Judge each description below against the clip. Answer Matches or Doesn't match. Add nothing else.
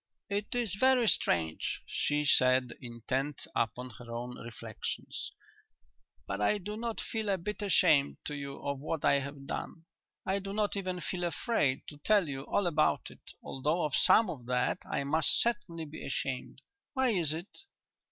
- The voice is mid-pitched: Matches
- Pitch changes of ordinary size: Doesn't match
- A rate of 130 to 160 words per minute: Doesn't match